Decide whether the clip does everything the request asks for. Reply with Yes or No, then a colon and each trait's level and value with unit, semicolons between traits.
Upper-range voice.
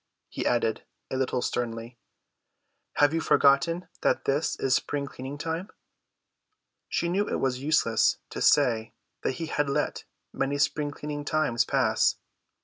No: medium, 140 Hz